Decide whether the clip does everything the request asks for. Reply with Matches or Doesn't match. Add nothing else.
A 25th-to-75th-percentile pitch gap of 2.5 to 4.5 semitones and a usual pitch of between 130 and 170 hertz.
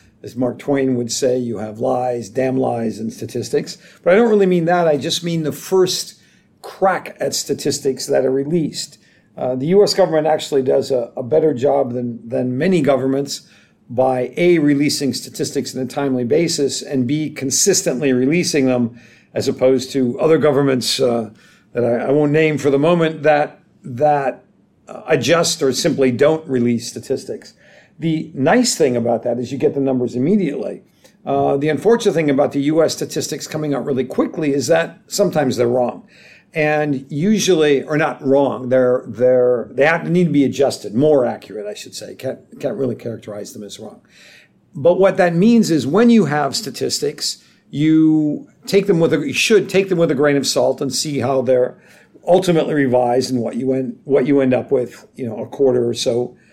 Matches